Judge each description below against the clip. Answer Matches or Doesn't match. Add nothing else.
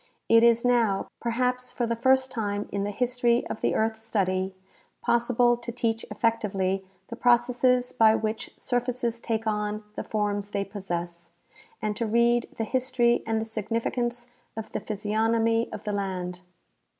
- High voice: Matches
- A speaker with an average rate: Matches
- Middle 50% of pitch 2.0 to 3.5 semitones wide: Matches